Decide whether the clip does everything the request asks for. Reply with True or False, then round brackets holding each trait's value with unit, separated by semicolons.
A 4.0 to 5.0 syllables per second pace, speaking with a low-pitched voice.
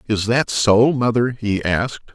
True (4.1 syllables/s; 115 Hz)